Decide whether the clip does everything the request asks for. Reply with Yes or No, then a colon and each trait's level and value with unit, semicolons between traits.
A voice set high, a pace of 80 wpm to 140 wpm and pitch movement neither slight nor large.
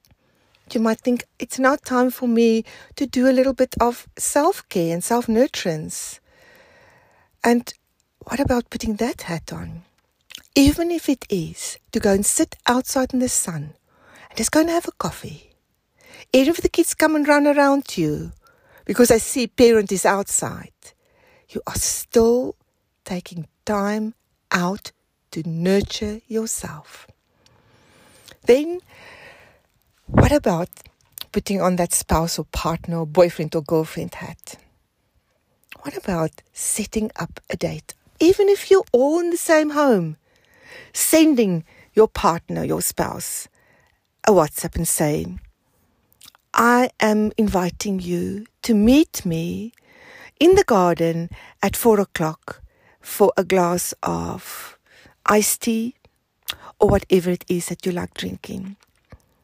No: high, 220 Hz; slow, 135 wpm; wide, 7.2 semitones